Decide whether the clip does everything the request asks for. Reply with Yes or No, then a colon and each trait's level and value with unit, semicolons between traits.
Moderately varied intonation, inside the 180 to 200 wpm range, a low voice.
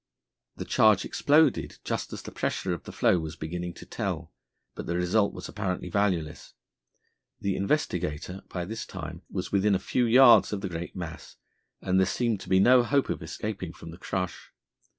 Yes: average, 3.7 semitones; average, 185 wpm; very low, 95 Hz